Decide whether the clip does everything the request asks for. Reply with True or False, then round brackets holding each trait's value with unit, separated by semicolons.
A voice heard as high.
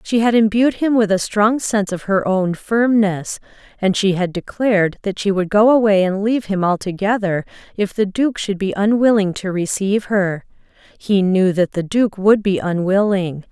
True (200 Hz)